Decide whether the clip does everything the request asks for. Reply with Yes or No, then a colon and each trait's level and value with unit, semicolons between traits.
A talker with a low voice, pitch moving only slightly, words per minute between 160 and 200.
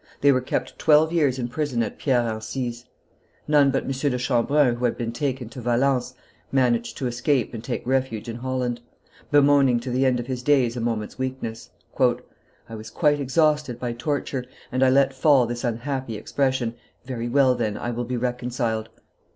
Yes: low, 125 Hz; narrow, 2.3 semitones; average, 185 wpm